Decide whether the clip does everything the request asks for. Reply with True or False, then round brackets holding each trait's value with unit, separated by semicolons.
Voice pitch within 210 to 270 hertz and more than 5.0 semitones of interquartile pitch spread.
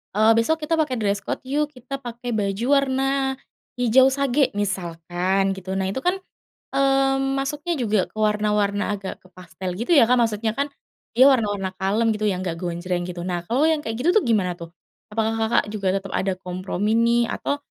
True (215 Hz; 5.5 semitones)